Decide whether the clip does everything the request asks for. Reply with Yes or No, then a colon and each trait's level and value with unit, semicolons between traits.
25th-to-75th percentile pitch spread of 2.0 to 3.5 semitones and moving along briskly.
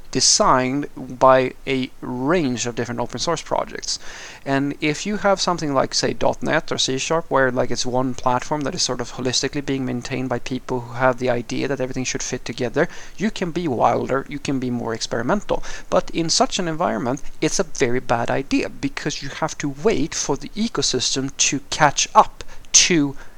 No: average, 3.0 semitones; average, 190 wpm